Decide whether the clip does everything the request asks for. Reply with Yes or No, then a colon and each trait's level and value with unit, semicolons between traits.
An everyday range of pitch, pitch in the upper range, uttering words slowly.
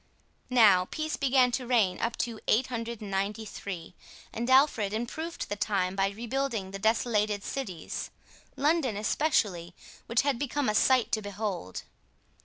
Yes: average, 4.4 semitones; high, 225 Hz; slow, 130 wpm